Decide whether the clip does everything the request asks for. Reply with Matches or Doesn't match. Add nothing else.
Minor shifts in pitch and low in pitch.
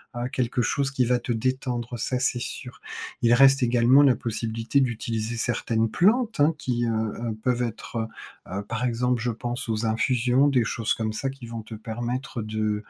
Matches